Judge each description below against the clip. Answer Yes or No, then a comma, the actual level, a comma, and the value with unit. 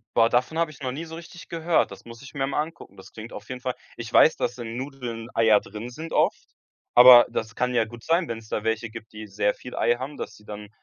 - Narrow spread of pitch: No, average, 3.7 semitones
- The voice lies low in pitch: Yes, low, 120 Hz